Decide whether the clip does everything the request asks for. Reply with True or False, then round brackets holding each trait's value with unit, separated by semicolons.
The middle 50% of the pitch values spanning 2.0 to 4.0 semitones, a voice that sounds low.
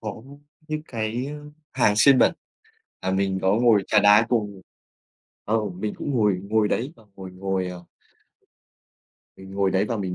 True (3.2 semitones; 105 Hz)